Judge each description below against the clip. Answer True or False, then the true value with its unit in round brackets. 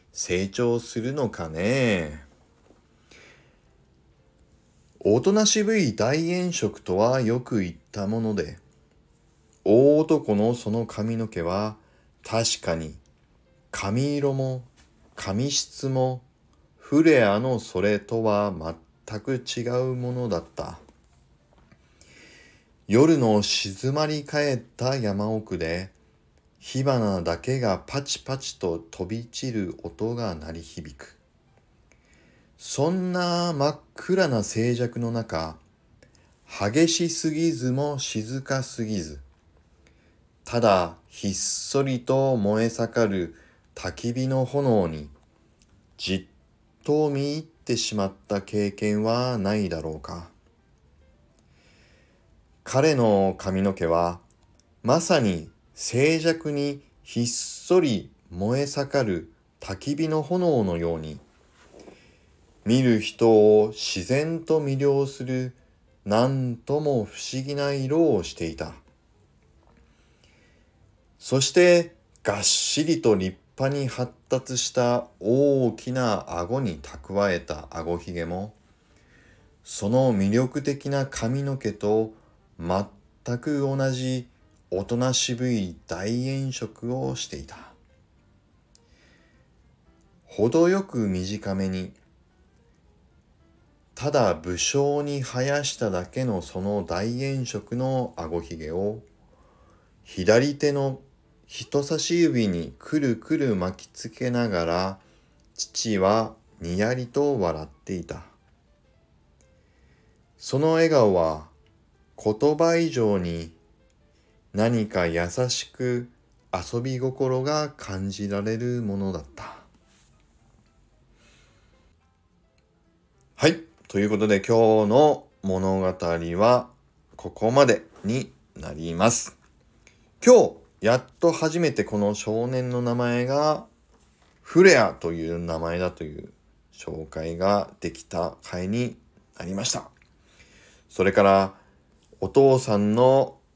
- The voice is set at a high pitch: False (110 Hz)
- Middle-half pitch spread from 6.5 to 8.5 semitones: True (7.0 semitones)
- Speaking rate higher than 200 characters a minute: False (175 characters per minute)